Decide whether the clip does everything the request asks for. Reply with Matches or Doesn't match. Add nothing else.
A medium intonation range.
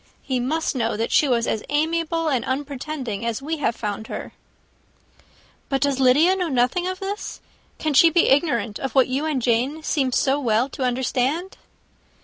Matches